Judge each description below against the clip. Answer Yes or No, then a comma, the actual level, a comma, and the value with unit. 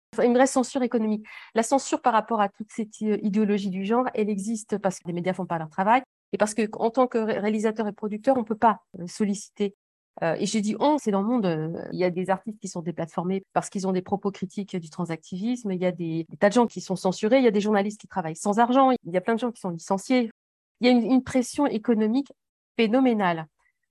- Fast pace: Yes, fast, 255 wpm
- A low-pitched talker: No, high, 210 Hz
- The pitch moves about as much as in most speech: Yes, average, 3.9 semitones